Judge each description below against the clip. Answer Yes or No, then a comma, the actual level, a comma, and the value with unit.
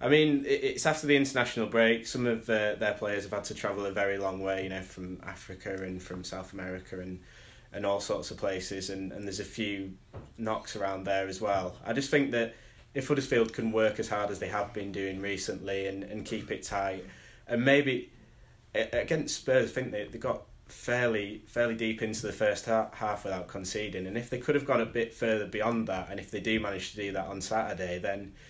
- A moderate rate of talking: No, fast, 225 wpm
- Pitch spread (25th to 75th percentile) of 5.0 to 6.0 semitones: No, average, 3.0 semitones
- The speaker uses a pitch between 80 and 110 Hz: Yes, low, 105 Hz